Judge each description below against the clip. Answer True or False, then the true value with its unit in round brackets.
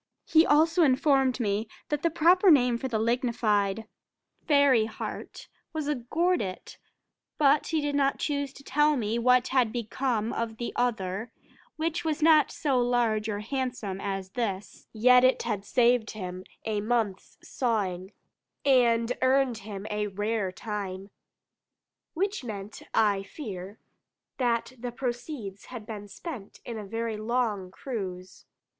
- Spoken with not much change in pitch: False (4.6 semitones)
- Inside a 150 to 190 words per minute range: False (140 wpm)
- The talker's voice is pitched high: True (235 Hz)